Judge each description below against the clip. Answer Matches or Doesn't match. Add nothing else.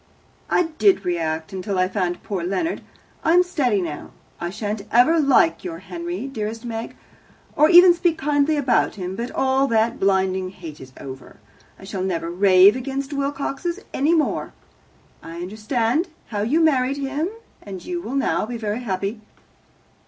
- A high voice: Matches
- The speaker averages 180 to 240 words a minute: Doesn't match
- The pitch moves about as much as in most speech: Doesn't match